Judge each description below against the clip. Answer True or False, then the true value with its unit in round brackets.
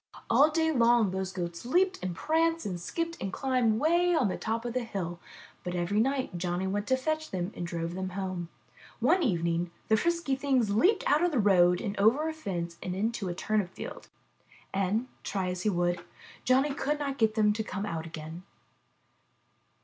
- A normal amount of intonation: False (7.2 semitones)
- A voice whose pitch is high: True (210 Hz)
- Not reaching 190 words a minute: False (195 wpm)